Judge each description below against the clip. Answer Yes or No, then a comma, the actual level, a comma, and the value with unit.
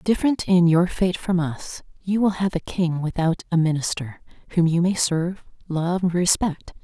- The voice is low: No, medium, 175 Hz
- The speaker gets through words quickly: No, average, 175 wpm